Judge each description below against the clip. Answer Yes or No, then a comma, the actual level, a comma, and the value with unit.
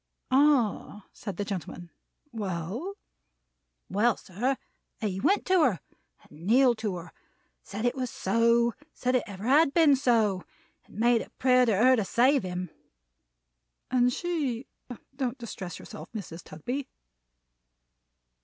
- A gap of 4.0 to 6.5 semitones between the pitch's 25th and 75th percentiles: Yes, average, 5.0 semitones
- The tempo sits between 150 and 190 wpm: No, slow, 135 wpm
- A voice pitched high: Yes, high, 235 Hz